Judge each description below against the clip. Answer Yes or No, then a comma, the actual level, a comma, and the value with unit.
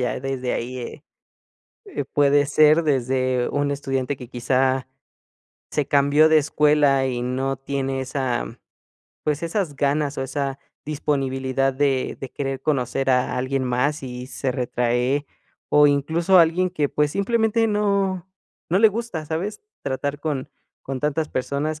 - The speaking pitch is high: No, medium, 140 Hz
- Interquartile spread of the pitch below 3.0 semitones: Yes, narrow, 2.6 semitones